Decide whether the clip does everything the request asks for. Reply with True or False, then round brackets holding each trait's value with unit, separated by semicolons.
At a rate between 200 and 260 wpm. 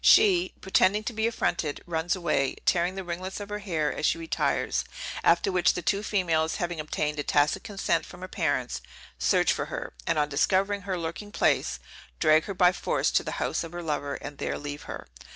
True (205 wpm)